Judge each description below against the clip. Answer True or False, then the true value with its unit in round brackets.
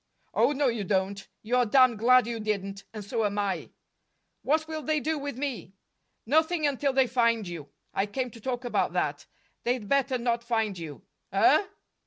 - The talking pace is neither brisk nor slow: True (180 wpm)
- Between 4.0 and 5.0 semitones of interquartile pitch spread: True (4.6 semitones)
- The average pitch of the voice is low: False (240 Hz)